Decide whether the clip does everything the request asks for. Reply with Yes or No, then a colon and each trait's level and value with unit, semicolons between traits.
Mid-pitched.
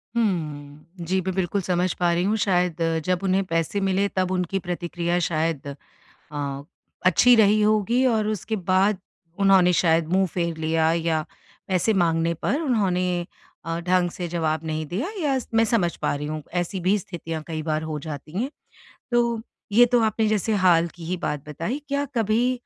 Yes: medium, 180 Hz